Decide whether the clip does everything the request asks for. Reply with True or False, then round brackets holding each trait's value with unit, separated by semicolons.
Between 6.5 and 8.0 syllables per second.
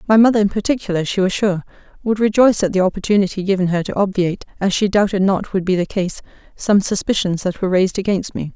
True (6.7 syllables/s)